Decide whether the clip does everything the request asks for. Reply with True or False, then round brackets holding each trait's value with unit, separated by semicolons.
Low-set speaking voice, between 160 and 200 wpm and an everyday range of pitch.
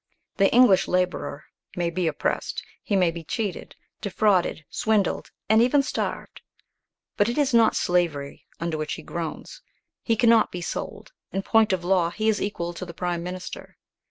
False (185 Hz; 165 wpm; 4.2 semitones)